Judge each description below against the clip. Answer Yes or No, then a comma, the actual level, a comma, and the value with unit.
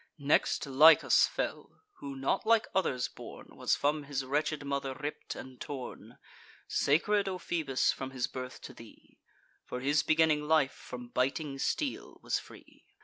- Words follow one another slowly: No, average, 150 wpm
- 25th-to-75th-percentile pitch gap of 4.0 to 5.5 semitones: No, average, 2.9 semitones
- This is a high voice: No, medium, 145 Hz